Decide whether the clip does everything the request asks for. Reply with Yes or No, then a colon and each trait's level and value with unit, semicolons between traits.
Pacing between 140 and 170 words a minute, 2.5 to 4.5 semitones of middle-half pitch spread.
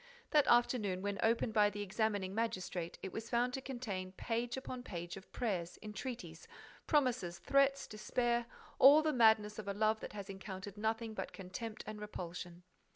Yes: average, 165 wpm; average, 4.0 semitones